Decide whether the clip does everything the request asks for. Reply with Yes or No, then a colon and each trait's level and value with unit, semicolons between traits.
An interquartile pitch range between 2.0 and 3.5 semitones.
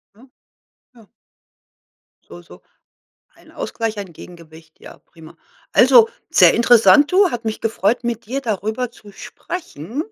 No: average, 4.0 semitones